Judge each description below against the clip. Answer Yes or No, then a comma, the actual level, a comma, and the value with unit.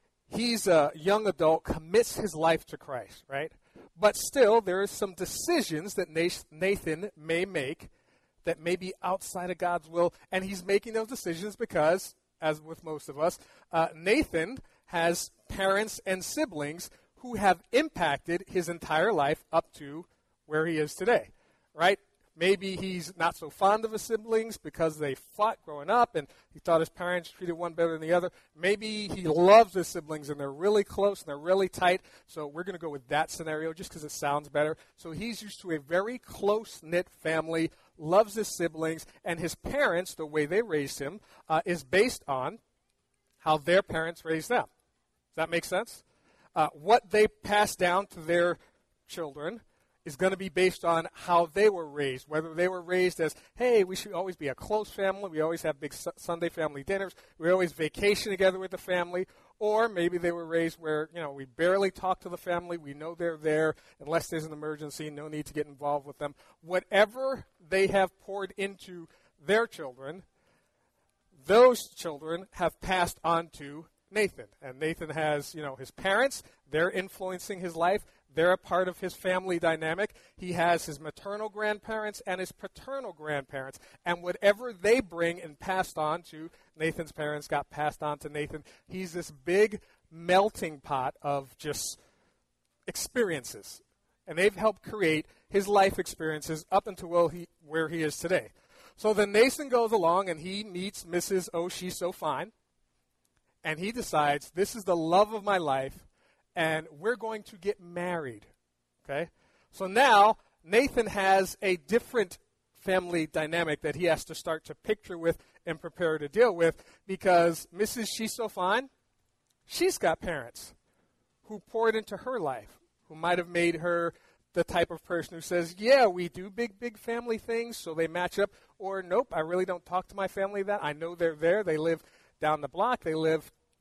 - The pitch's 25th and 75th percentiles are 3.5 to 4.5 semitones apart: Yes, average, 3.8 semitones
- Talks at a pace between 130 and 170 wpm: No, average, 180 wpm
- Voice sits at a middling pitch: Yes, medium, 175 Hz